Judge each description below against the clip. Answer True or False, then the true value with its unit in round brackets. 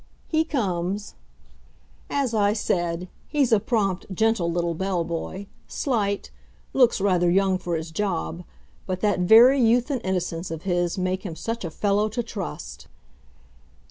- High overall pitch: True (195 Hz)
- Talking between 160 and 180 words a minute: False (145 wpm)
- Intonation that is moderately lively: True (4.2 semitones)